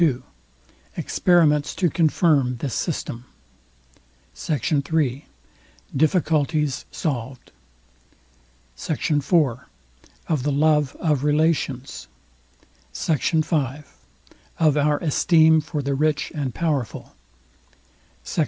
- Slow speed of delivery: Yes, slow, 90 wpm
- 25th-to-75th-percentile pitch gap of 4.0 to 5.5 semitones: No, narrow, 2.5 semitones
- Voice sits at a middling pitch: Yes, medium, 150 Hz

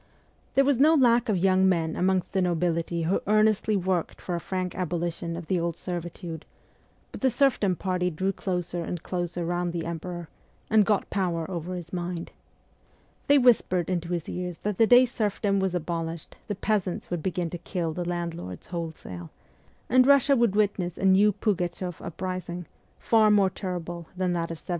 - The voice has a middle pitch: Yes, medium, 180 Hz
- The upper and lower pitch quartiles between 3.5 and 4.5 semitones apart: No, average, 2.8 semitones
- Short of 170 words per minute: No, average, 175 wpm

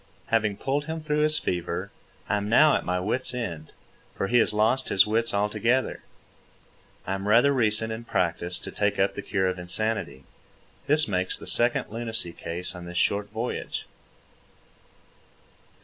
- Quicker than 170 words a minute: No, average, 165 wpm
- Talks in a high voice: No, low, 105 Hz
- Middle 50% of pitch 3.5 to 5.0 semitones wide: Yes, average, 4.3 semitones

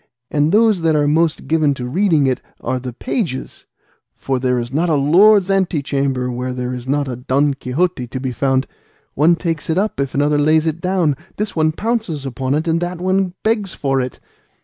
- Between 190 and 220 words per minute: Yes, average, 200 wpm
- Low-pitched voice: No, medium, 150 Hz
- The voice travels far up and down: No, average, 4.7 semitones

